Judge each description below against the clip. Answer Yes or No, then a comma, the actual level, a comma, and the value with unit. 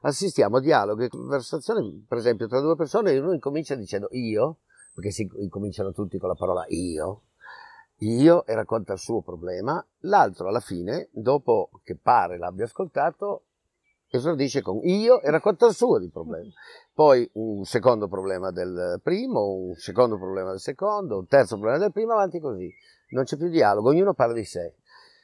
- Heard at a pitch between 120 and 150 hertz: Yes, medium, 140 Hz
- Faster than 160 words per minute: Yes, fast, 170 wpm